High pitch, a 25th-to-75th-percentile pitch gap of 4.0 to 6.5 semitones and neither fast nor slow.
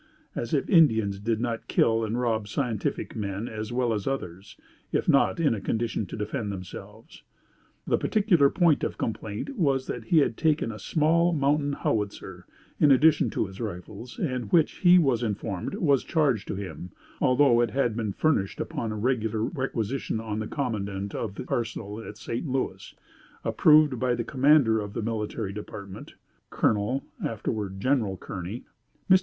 No: low, 115 Hz; average, 4.9 semitones; average, 165 wpm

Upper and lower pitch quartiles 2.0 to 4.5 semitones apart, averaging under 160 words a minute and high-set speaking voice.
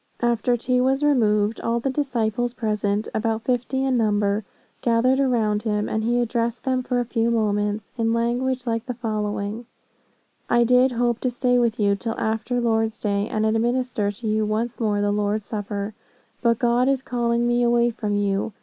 No: narrow, 2.4 semitones; average, 180 wpm; high, 230 Hz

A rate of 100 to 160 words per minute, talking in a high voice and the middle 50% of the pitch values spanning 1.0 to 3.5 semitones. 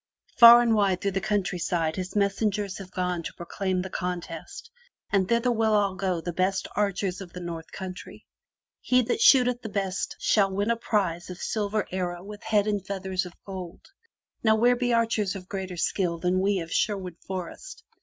No: average, 195 wpm; high, 195 Hz; average, 2.8 semitones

